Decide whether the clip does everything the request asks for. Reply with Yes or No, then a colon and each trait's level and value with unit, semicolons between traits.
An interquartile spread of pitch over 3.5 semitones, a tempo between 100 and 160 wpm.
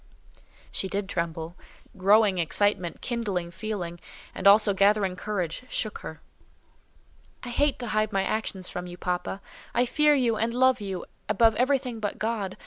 Yes: average, 3.9 semitones; average, 150 wpm